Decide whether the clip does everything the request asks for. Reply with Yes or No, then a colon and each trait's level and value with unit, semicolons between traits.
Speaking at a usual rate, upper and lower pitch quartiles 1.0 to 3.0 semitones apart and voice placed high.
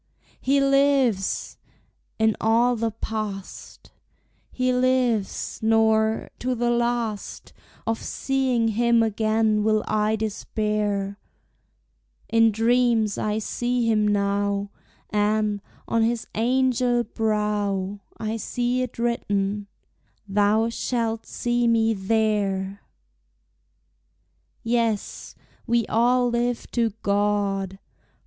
No: slow, 95 wpm; narrow, 2.4 semitones; high, 220 Hz